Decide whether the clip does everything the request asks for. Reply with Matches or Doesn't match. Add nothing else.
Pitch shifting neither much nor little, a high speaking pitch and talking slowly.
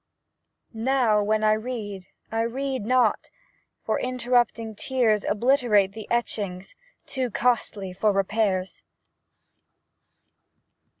Matches